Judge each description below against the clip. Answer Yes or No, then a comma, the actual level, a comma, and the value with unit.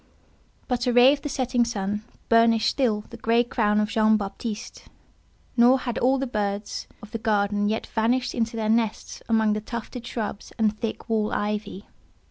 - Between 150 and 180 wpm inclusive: Yes, average, 175 wpm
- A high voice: Yes, high, 225 Hz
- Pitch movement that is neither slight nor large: No, narrow, 2.3 semitones